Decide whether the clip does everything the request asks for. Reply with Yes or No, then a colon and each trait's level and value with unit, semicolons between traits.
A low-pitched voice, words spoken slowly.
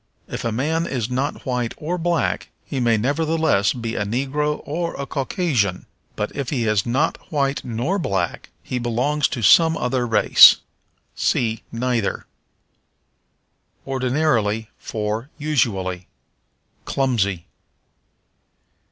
Yes: low, 125 Hz; slow, 115 wpm